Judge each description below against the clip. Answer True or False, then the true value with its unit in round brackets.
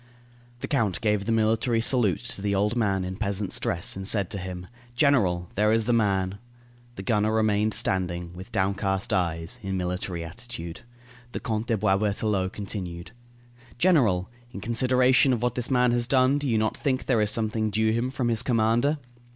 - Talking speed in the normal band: True (180 wpm)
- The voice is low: True (105 Hz)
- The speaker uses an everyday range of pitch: True (3.8 semitones)